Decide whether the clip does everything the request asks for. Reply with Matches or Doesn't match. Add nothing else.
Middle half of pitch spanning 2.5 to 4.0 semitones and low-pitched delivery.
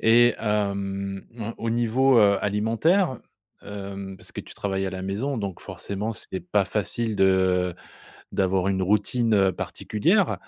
Matches